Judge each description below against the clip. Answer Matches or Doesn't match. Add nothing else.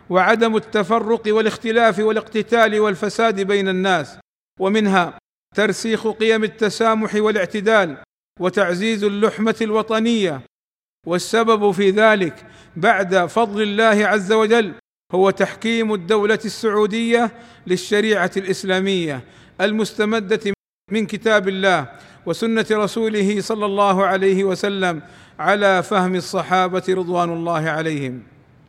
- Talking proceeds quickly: Doesn't match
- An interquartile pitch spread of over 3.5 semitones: Doesn't match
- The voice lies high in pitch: Matches